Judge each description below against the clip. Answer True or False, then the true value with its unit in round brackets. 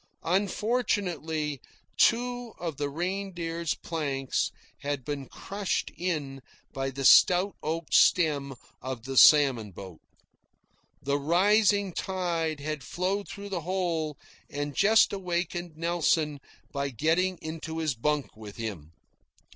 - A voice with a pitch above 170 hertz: False (160 Hz)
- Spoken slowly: True (115 wpm)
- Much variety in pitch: False (4.7 semitones)